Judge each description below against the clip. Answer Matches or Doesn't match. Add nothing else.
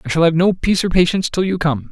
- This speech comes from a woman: Doesn't match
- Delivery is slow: Doesn't match